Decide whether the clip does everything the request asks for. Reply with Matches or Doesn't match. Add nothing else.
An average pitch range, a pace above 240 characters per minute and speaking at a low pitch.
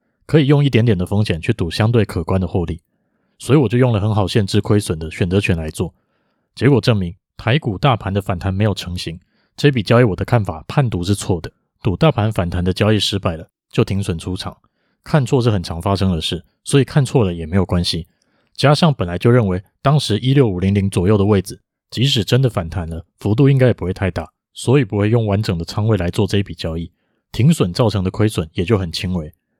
Matches